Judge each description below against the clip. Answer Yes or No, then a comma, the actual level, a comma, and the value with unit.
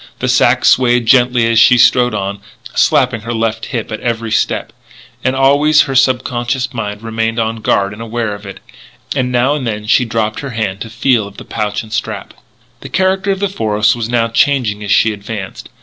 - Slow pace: No, average, 200 wpm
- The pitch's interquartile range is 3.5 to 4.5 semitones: No, average, 2.8 semitones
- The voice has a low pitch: Yes, low, 115 Hz